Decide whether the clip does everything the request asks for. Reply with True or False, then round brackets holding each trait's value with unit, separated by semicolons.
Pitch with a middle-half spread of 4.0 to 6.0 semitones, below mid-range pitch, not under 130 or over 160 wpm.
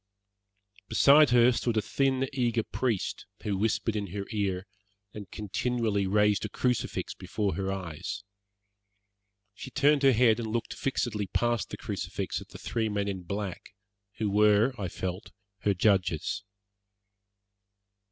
False (3.2 semitones; 105 Hz; 140 wpm)